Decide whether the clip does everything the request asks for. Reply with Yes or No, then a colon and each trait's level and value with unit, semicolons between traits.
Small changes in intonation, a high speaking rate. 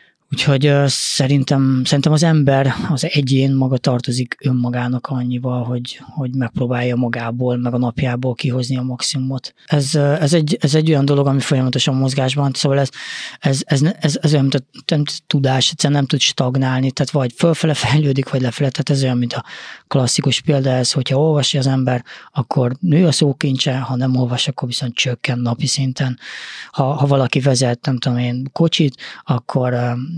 Yes: narrow, 2.3 semitones; fast, 165 wpm